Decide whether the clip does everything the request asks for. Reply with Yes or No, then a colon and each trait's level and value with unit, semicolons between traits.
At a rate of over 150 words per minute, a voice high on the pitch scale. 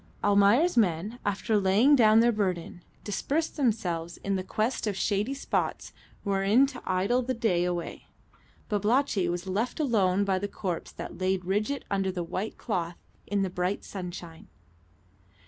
No: average, 145 wpm; high, 200 Hz